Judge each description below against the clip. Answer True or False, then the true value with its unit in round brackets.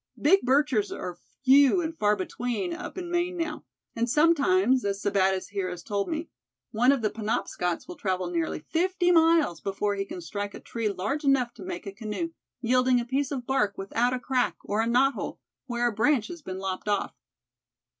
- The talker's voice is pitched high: True (240 Hz)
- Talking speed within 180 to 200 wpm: True (195 wpm)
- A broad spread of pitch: True (6.8 semitones)